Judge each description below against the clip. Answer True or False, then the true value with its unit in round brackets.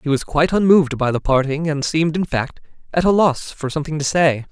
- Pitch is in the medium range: True (155 Hz)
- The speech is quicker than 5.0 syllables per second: True (6.1 syllables/s)